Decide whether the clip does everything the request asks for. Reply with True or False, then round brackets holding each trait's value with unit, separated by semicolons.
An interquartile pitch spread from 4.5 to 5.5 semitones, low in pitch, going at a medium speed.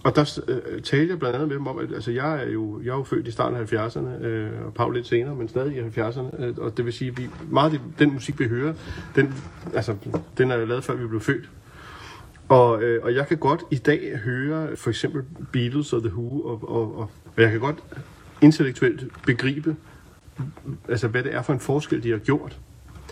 False (3.8 semitones; 130 Hz; 215 wpm)